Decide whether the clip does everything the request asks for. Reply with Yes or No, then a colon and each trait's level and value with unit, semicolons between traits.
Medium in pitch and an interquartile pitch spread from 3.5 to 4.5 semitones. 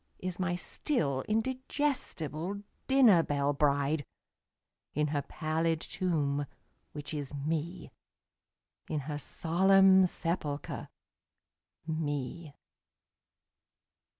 Yes: medium, 160 Hz; average, 4.2 semitones